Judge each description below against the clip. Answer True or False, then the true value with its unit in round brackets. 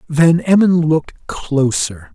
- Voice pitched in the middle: True (155 Hz)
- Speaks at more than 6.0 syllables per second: False (3.5 syllables/s)